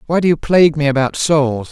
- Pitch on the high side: No, medium, 150 Hz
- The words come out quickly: Yes, fast, 245 wpm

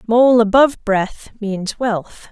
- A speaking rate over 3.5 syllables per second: No, 3.4 syllables/s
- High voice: Yes, high, 220 Hz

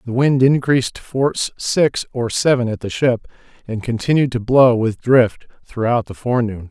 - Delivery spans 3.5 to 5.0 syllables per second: Yes, 4.9 syllables/s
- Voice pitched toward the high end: No, low, 125 Hz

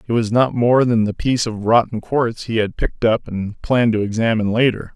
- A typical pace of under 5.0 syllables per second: No, 5.6 syllables/s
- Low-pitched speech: Yes, low, 115 Hz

